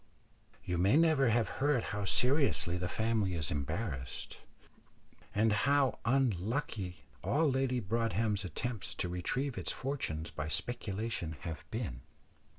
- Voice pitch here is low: Yes, low, 110 Hz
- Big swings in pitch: Yes, wide, 6.5 semitones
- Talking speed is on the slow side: Yes, slow, 125 wpm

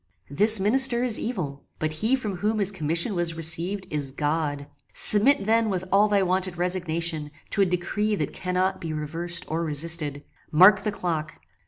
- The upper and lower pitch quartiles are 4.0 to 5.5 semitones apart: Yes, average, 4.4 semitones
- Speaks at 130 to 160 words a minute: No, average, 170 wpm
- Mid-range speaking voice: Yes, medium, 180 Hz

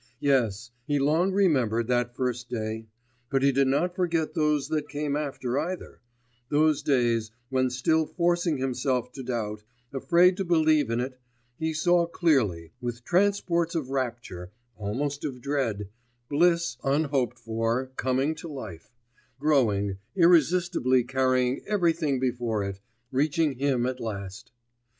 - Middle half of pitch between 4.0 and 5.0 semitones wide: Yes, average, 4.6 semitones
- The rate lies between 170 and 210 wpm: No, slow, 135 wpm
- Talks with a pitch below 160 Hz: Yes, low, 135 Hz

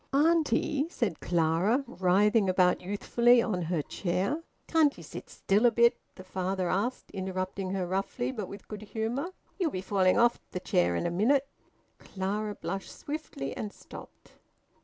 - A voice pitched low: No, high, 200 Hz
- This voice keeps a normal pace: Yes, average, 160 wpm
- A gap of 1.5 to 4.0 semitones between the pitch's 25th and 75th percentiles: No, average, 4.6 semitones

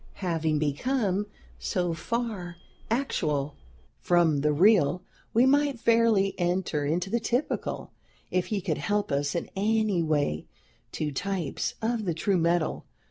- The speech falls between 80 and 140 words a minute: Yes, slow, 135 wpm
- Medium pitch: Yes, medium, 180 Hz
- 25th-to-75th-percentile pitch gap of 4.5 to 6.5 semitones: Yes, wide, 5.6 semitones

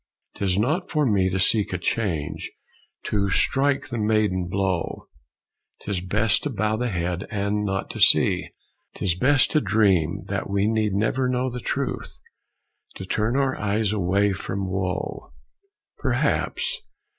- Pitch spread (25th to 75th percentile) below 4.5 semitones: Yes, average, 3.1 semitones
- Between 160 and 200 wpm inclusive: No, average, 145 wpm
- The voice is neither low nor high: No, low, 100 Hz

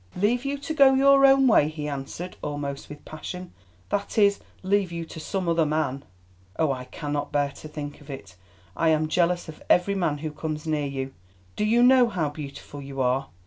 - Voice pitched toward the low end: No, medium, 155 Hz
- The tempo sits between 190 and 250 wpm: Yes, average, 195 wpm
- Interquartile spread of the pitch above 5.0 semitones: Yes, wide, 5.6 semitones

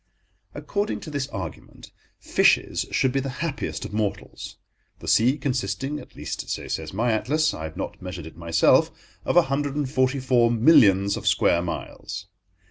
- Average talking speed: Yes, average, 160 wpm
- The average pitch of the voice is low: Yes, low, 125 Hz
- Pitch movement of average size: No, wide, 6.4 semitones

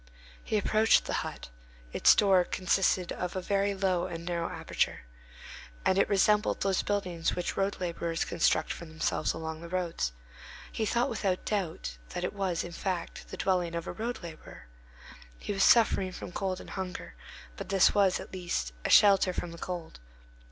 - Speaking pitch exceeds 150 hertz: Yes, medium, 185 Hz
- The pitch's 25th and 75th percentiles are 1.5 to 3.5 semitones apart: Yes, narrow, 2.6 semitones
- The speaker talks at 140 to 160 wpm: No, average, 175 wpm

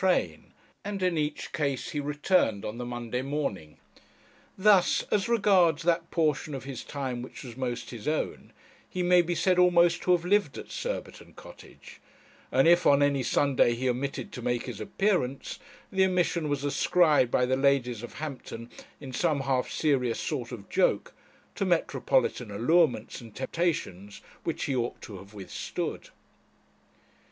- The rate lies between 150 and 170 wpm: Yes, average, 160 wpm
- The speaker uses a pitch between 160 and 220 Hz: No, medium, 140 Hz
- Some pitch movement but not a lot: No, wide, 5.9 semitones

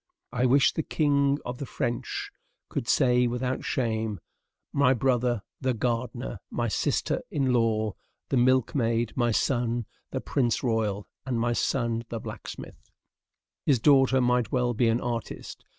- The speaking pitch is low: Yes, low, 120 Hz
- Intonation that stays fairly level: Yes, narrow, 2.1 semitones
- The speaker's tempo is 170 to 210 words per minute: No, average, 150 wpm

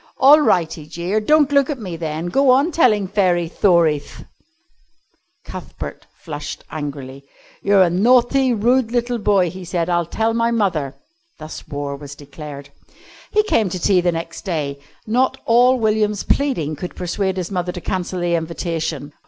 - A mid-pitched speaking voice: Yes, medium, 180 Hz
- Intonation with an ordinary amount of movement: No, wide, 6.3 semitones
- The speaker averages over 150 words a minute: Yes, average, 160 wpm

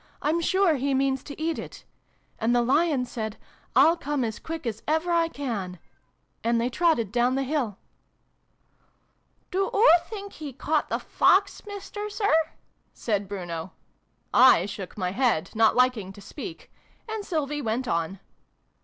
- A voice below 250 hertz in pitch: No, very high, 265 Hz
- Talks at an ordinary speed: Yes, average, 165 wpm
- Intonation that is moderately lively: No, wide, 6.9 semitones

